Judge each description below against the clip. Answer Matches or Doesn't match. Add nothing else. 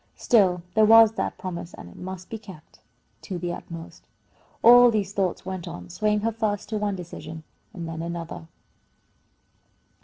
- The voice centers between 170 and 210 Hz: Matches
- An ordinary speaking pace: Matches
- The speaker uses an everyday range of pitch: Matches